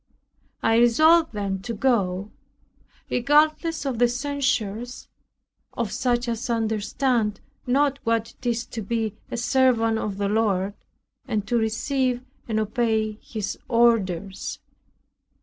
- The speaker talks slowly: Yes, slow, 120 wpm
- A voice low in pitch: No, high, 230 Hz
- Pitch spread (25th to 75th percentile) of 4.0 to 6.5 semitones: No, average, 2.9 semitones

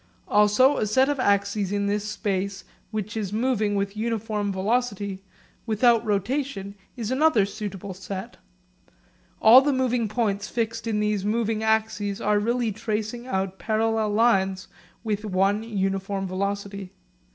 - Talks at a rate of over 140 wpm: No, slow, 135 wpm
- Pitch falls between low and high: No, high, 210 Hz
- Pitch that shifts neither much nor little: No, narrow, 2.3 semitones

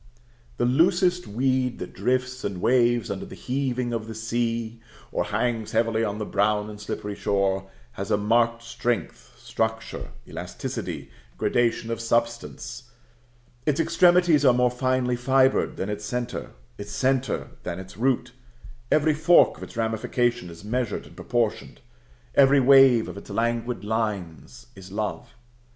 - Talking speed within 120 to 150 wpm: Yes, average, 145 wpm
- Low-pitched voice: Yes, low, 120 Hz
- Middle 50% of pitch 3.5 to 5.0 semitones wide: No, average, 3.1 semitones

